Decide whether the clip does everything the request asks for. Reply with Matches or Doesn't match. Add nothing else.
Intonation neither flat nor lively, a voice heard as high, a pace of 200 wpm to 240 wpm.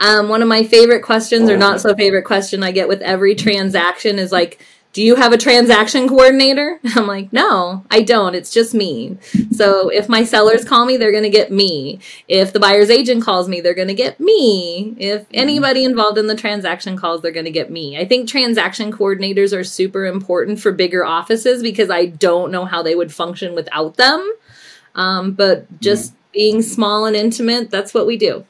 Matches